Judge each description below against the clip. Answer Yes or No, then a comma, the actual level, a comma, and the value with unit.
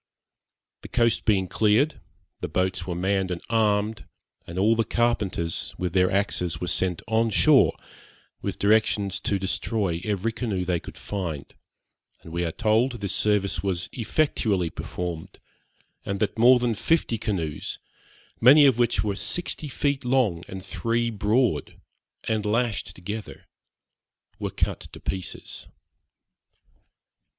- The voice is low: Yes, low, 105 Hz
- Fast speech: No, slow, 135 wpm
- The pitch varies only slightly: No, average, 3.9 semitones